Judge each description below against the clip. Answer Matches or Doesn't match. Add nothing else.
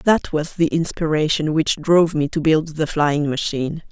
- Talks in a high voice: Doesn't match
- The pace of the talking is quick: Doesn't match